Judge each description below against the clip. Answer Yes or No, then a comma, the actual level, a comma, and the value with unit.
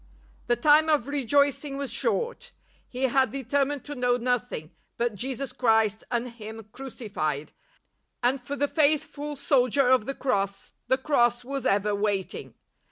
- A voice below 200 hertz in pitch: No, very high, 250 Hz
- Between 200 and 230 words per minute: No, average, 150 wpm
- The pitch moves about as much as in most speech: Yes, average, 3.9 semitones